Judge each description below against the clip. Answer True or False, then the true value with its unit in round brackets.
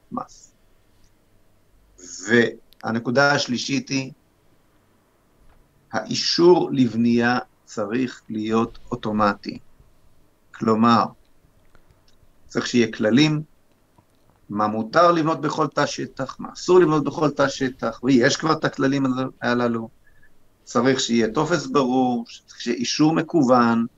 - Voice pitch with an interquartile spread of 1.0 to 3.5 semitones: False (4.0 semitones)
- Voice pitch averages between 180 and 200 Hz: False (120 Hz)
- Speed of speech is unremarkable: False (90 wpm)